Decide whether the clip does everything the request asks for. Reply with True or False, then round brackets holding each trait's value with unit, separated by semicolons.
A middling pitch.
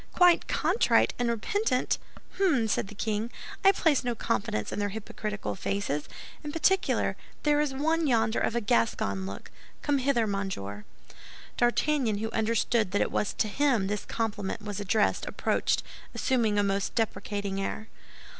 False (220 Hz)